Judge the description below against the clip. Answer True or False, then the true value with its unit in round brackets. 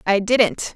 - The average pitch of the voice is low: False (215 Hz)